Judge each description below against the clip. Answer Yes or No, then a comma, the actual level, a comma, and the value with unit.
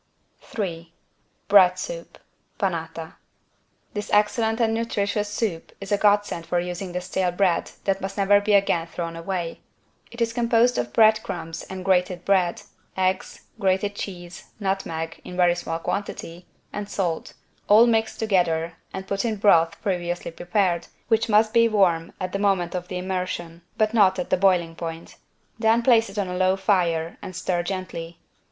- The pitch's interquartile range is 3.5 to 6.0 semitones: No, average, 3.0 semitones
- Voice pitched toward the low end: No, high, 190 Hz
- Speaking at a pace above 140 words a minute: Yes, average, 165 wpm